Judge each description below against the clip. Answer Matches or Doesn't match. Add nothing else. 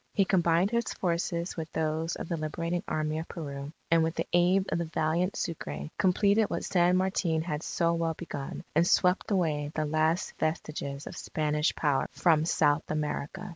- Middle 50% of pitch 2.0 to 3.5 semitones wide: Matches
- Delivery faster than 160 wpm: Matches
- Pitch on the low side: Doesn't match